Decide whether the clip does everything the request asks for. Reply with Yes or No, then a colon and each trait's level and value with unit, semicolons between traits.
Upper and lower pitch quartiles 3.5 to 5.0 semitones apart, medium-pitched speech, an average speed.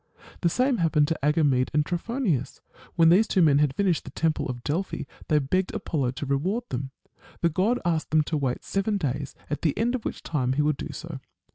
No: average, 4.7 semitones; medium, 155 Hz; fast, 215 wpm